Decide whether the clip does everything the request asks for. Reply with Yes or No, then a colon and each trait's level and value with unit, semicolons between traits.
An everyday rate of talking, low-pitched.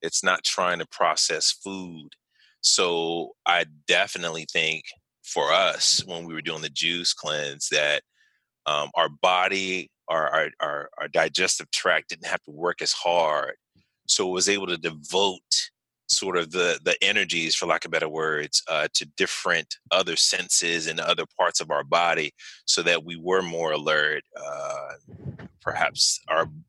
Yes: average, 155 wpm; very low, 85 Hz